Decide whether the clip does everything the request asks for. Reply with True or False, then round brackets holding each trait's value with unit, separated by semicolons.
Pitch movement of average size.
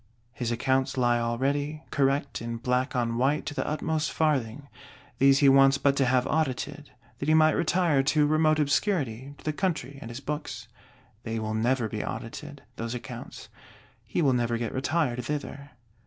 True (3.7 semitones)